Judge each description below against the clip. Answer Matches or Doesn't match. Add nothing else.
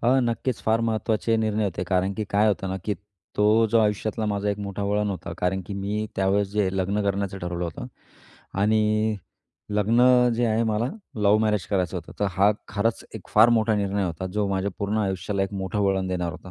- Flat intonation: Matches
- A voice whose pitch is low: Matches